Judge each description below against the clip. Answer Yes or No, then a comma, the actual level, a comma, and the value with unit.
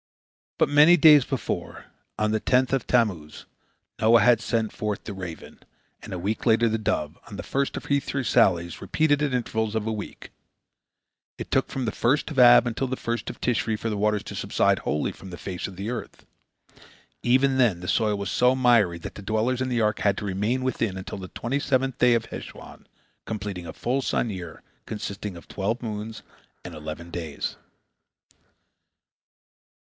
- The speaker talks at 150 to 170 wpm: No, average, 190 wpm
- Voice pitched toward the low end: Yes, low, 110 Hz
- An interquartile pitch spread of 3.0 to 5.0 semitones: Yes, average, 4.0 semitones